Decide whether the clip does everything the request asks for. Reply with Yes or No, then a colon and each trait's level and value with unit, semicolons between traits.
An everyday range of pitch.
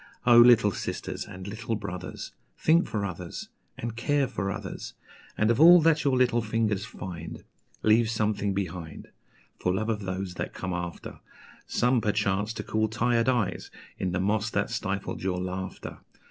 Yes: average, 3.7 semitones